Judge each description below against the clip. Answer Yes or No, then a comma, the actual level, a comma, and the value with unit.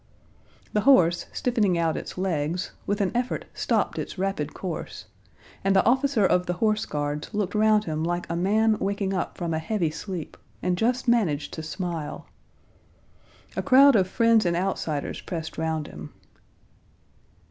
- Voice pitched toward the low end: No, medium, 185 Hz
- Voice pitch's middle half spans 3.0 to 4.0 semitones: No, average, 4.7 semitones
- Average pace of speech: Yes, average, 160 wpm